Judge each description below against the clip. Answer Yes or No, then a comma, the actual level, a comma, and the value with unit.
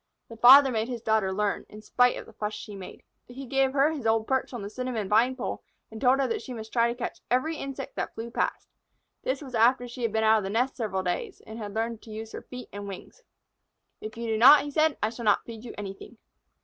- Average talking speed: No, fast, 255 wpm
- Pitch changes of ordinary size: Yes, average, 3.0 semitones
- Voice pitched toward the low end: No, high, 230 Hz